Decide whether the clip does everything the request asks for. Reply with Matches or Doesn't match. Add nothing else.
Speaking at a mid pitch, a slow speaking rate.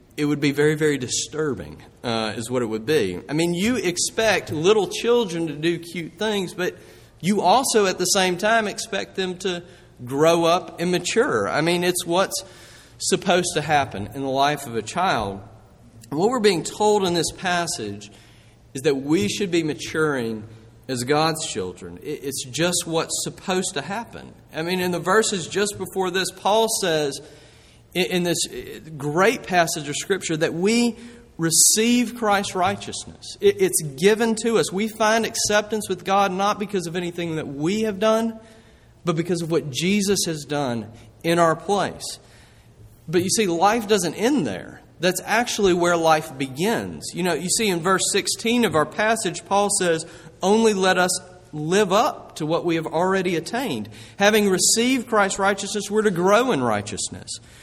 Doesn't match